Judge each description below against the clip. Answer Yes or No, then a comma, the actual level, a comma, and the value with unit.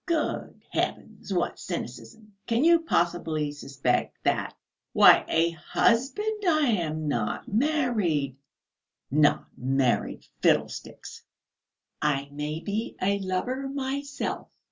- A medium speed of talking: No, slow, 100 wpm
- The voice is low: No, high, 190 Hz